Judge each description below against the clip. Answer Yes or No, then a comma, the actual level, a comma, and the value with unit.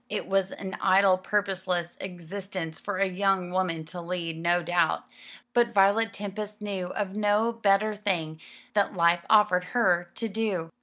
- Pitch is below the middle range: No, high, 190 Hz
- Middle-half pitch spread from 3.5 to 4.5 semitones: No, average, 2.8 semitones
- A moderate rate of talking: Yes, average, 155 wpm